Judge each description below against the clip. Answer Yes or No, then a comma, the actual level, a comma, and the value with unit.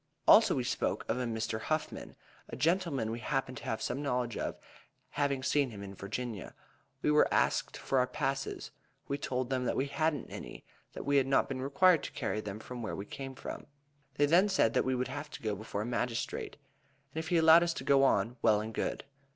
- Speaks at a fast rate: Yes, fast, 220 wpm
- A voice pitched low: Yes, low, 130 Hz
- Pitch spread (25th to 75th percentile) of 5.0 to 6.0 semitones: No, average, 4.1 semitones